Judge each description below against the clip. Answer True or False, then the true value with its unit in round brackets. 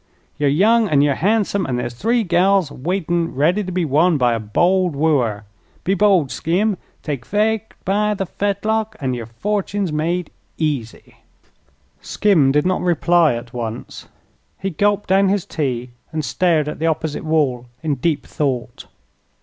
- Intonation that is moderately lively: False (5.9 semitones)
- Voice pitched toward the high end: False (165 Hz)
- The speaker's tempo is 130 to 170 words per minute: True (160 wpm)